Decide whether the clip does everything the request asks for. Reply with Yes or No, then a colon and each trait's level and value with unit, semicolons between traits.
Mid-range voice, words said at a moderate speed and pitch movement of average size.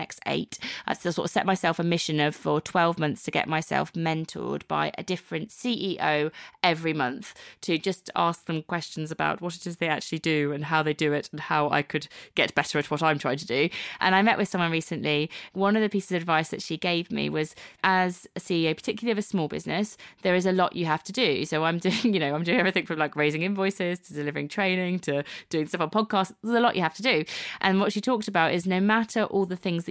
No: medium, 170 Hz; fast, 250 wpm; average, 3.7 semitones